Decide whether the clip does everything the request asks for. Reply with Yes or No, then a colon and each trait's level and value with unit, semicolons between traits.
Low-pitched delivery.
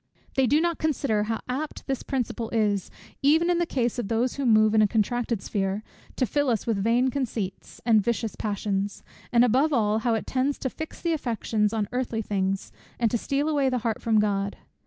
No: high, 230 Hz